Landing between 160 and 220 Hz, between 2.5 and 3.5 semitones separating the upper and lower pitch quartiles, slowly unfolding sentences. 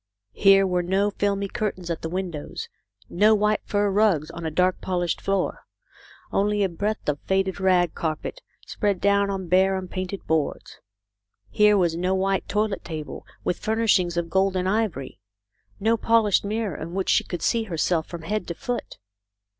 No: high, 190 Hz; average, 2.8 semitones; average, 170 wpm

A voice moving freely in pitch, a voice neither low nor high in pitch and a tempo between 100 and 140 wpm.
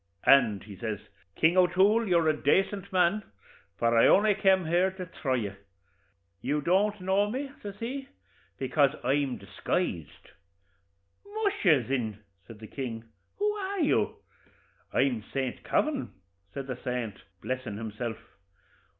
Yes: wide, 8.9 semitones; medium, 155 Hz; slow, 135 wpm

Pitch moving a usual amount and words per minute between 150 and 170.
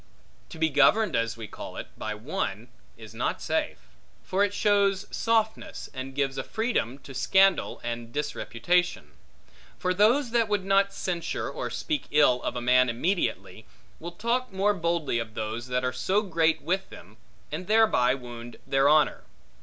No: wide, 8.0 semitones; average, 165 wpm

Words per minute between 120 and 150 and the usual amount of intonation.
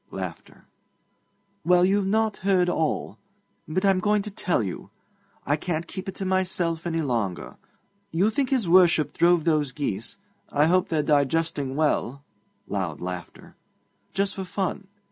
Yes: average, 145 wpm; average, 4.6 semitones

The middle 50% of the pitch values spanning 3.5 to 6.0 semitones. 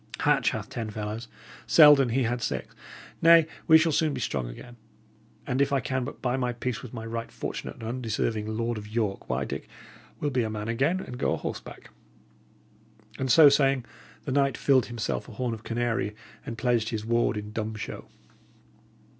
No: average, 3.1 semitones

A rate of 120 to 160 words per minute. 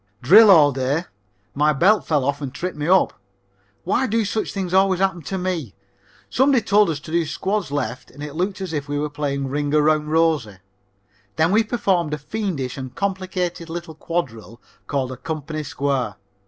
No: average, 180 wpm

